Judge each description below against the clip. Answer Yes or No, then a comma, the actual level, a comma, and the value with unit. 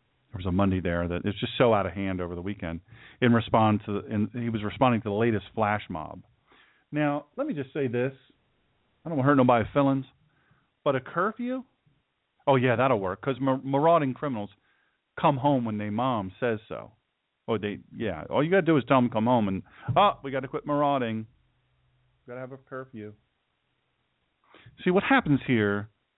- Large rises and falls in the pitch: No, average, 4.8 semitones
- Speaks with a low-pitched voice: Yes, low, 125 Hz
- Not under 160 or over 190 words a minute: No, average, 200 wpm